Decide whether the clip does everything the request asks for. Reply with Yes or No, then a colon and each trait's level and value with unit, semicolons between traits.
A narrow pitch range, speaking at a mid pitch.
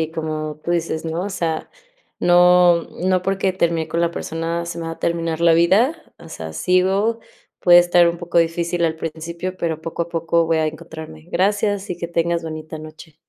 Yes: narrow, 1.6 semitones; medium, 170 Hz